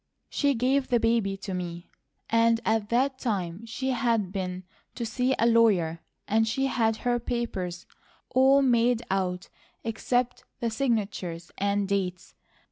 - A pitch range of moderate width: Yes, average, 4.0 semitones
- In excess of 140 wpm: No, slow, 135 wpm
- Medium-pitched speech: No, high, 225 Hz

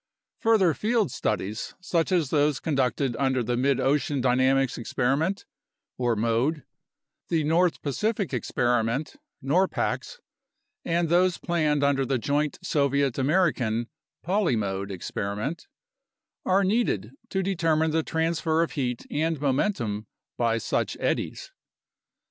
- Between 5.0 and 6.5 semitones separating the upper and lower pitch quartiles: Yes, wide, 5.4 semitones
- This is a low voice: No, medium, 145 Hz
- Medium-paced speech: No, slow, 115 wpm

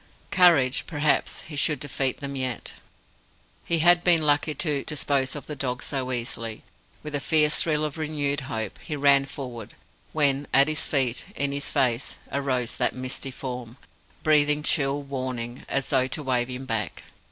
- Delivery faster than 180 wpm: No, average, 165 wpm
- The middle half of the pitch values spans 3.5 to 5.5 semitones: No, average, 2.7 semitones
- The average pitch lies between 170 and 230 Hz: No, medium, 140 Hz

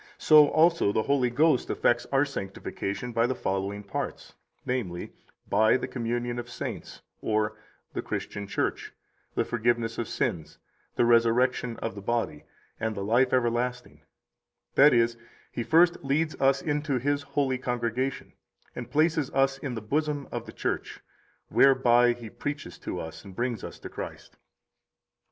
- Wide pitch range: No, average, 3.2 semitones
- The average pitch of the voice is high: No, low, 120 Hz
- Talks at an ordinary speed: Yes, average, 150 wpm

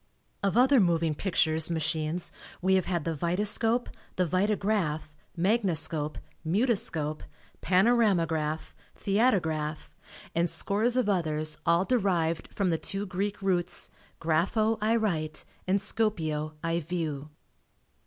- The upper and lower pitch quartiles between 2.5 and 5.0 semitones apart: Yes, average, 4.4 semitones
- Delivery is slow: Yes, slow, 110 wpm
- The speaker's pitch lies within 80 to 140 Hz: No, medium, 180 Hz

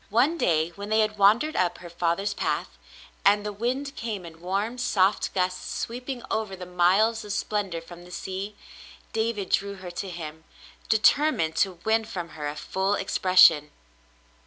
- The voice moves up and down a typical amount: Yes, average, 3.8 semitones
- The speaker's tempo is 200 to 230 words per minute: No, average, 165 wpm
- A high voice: Yes, high, 195 Hz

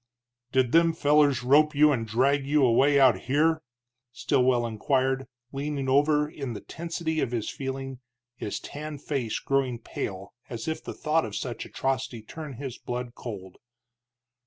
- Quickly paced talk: No, average, 155 wpm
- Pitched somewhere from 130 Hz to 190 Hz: Yes, low, 135 Hz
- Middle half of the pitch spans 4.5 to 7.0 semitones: No, average, 3.5 semitones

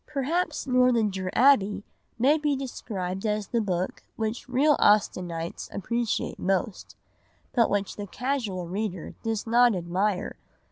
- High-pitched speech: Yes, high, 215 Hz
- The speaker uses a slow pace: Yes, slow, 125 wpm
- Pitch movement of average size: Yes, average, 4.8 semitones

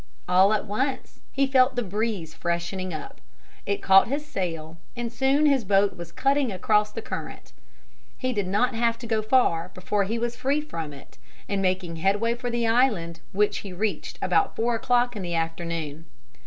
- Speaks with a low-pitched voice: No, high, 210 Hz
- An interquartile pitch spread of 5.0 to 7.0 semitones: Yes, average, 5.3 semitones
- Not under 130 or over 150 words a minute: No, average, 180 wpm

